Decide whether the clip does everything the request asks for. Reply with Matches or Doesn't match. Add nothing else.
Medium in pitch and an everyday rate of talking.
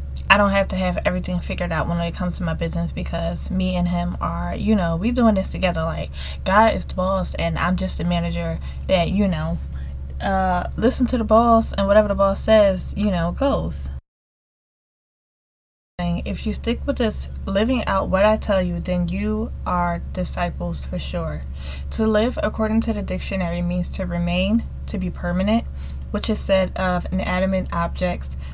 Matches